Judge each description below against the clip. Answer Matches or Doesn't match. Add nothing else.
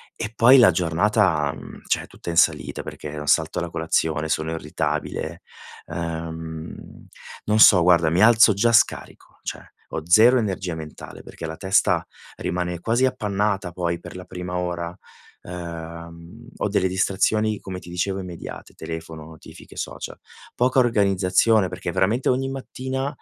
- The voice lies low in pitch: Matches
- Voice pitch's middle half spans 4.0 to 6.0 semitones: Matches